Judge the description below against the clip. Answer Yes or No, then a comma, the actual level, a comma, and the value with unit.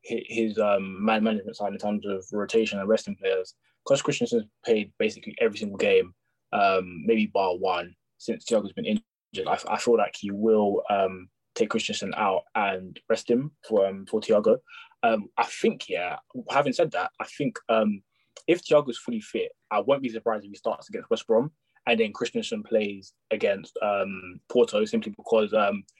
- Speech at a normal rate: Yes, average, 180 wpm